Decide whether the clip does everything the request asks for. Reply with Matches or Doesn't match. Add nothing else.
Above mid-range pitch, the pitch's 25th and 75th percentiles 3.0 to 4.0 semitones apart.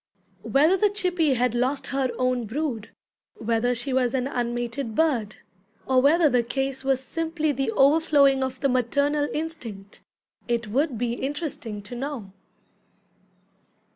Matches